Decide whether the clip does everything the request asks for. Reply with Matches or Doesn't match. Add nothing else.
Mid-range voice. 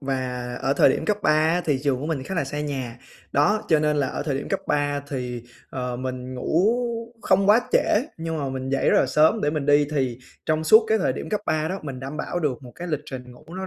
Matches